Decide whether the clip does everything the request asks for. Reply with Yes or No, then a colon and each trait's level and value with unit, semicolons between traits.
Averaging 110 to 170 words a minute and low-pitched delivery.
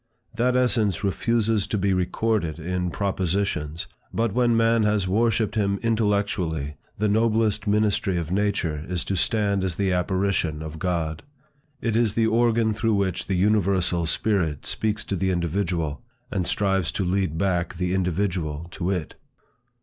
Yes: average, 150 wpm; very low, 95 Hz